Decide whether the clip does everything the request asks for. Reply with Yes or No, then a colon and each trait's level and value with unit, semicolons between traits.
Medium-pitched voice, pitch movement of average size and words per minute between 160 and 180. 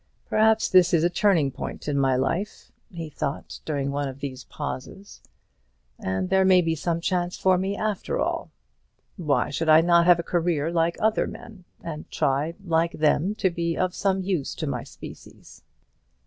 Yes: medium, 170 Hz; average, 3.8 semitones; average, 175 wpm